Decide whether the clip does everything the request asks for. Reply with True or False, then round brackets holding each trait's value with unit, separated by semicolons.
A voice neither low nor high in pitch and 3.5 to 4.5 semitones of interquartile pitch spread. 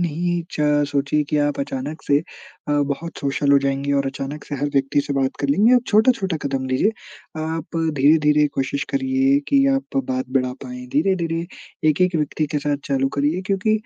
True (150 Hz; 3.8 semitones)